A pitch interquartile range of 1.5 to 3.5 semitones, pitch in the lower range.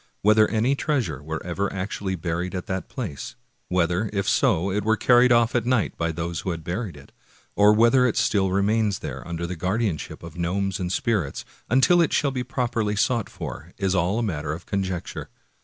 No: average, 4.8 semitones; low, 100 Hz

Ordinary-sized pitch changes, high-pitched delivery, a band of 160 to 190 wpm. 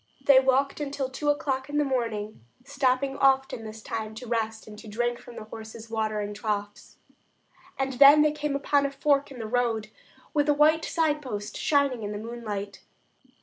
Yes: average, 4.3 semitones; very high, 255 Hz; average, 180 wpm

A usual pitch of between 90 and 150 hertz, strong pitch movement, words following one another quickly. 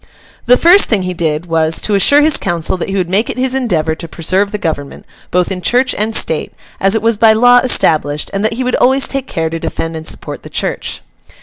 No: high, 195 Hz; wide, 6.9 semitones; fast, 235 wpm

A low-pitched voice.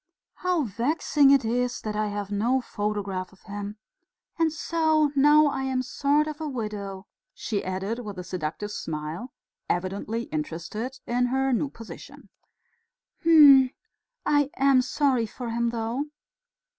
No: high, 235 Hz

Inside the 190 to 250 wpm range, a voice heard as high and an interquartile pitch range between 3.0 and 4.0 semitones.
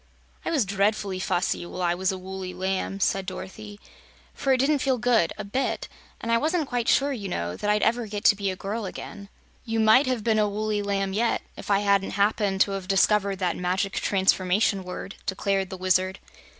No: fast, 205 wpm; high, 200 Hz; narrow, 2.6 semitones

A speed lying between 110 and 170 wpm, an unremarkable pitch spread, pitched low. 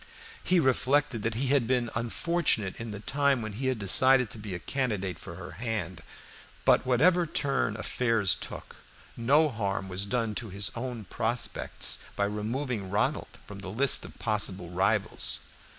Yes: average, 165 wpm; average, 4.4 semitones; low, 115 Hz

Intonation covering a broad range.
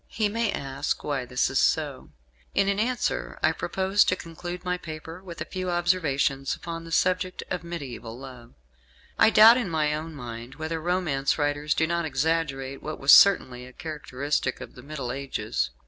No: average, 4.8 semitones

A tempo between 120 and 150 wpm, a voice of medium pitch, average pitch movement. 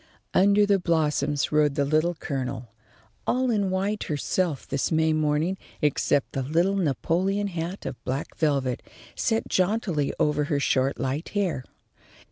Yes: average, 140 wpm; medium, 160 Hz; average, 4.9 semitones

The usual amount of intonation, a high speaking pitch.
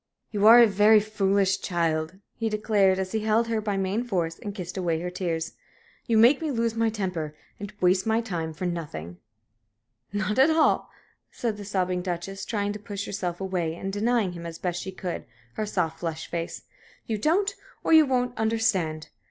Yes: average, 3.9 semitones; high, 195 Hz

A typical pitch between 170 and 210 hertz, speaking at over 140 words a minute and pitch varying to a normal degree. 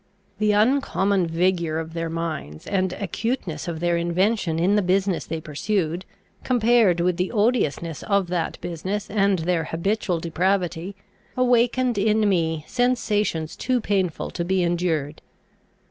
No: medium, 185 Hz; slow, 135 wpm; average, 3.9 semitones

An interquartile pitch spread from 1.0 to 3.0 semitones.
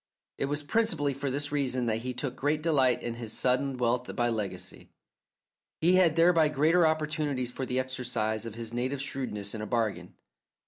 No: average, 3.8 semitones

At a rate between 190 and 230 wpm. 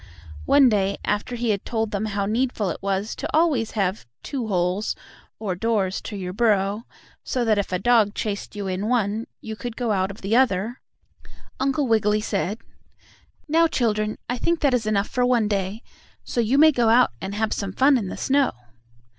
Yes: average, 195 wpm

